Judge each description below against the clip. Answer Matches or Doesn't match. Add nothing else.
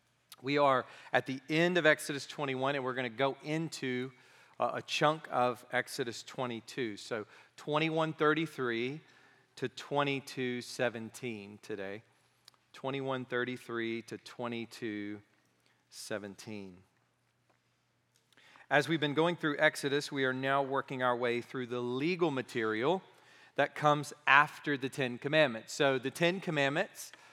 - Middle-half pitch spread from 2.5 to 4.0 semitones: Matches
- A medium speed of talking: Doesn't match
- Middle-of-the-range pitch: Doesn't match